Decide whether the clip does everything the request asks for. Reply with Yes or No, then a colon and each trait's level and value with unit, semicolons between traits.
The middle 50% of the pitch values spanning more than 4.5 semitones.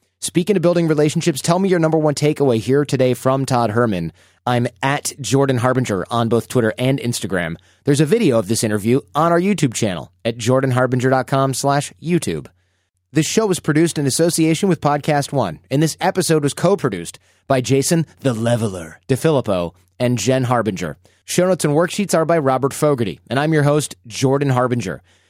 Yes: average, 5.0 semitones